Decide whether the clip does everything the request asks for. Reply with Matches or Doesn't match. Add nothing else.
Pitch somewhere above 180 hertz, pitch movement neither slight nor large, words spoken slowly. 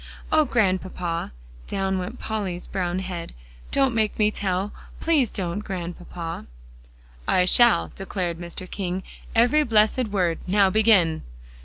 Matches